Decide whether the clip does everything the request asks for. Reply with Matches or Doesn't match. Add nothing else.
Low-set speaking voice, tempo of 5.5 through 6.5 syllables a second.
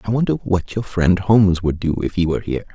Matches